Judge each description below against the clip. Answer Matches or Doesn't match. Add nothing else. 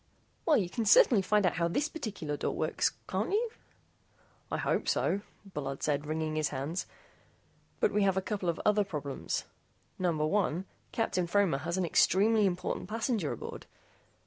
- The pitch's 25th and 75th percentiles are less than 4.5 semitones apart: Doesn't match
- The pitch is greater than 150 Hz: Matches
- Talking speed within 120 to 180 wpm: Matches